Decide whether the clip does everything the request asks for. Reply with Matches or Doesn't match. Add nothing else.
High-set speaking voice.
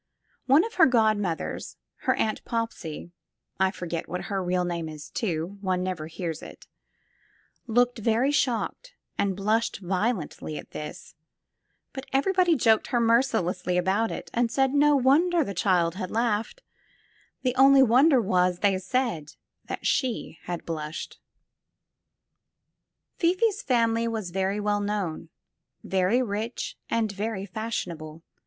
Matches